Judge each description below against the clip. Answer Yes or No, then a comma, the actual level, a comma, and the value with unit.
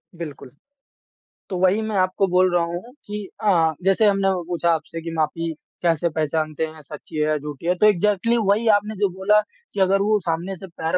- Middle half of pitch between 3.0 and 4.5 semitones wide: Yes, average, 3.7 semitones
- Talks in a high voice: No, medium, 180 Hz